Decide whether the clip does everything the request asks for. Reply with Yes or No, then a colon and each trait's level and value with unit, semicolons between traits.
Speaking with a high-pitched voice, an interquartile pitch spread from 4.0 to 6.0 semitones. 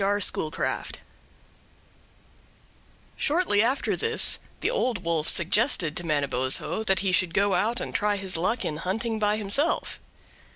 Yes: high, 200 Hz; average, 5.2 semitones